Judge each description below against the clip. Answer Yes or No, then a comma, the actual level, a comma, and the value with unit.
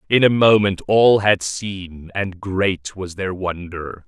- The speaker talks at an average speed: Yes, average, 160 wpm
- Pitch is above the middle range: No, very low, 95 Hz